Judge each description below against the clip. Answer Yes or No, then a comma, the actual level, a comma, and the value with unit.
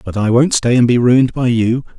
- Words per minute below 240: No, fast, 270 wpm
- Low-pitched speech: Yes, low, 120 Hz